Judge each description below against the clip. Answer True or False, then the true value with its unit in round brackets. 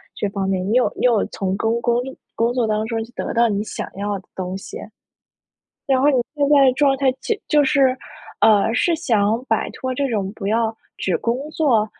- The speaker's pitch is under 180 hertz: False (235 Hz)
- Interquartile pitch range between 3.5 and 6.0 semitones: True (4.5 semitones)